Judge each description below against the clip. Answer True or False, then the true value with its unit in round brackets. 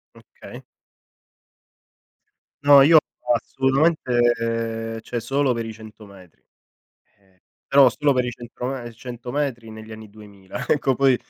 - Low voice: True (120 Hz)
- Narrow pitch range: False (3.3 semitones)